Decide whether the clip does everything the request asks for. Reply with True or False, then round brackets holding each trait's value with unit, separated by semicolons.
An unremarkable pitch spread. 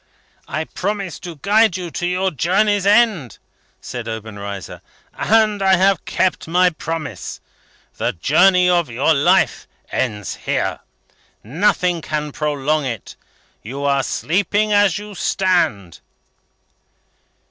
False (5.8 semitones)